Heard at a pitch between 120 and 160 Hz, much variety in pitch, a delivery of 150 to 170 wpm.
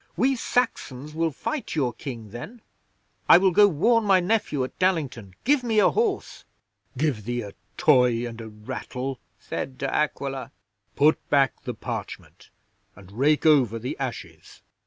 Yes: medium, 140 Hz; wide, 7.8 semitones; average, 155 wpm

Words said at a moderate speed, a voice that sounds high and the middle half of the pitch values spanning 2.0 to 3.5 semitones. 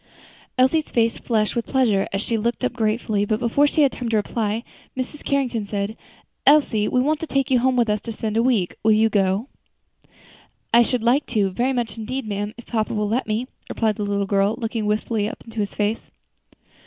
No: fast, 210 wpm; high, 225 Hz; average, 3.0 semitones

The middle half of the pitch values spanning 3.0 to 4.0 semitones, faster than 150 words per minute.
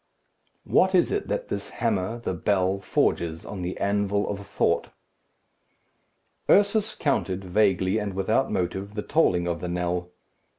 No: average, 3.7 semitones; average, 140 wpm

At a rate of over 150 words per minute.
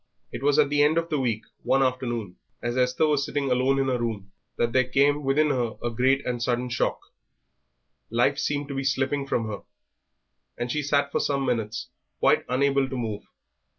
Yes: average, 195 wpm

